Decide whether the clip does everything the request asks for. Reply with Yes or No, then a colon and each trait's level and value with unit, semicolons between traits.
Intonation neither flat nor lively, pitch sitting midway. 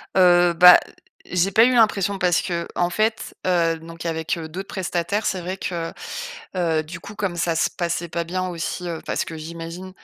No: narrow, 1.9 semitones; medium, 175 Hz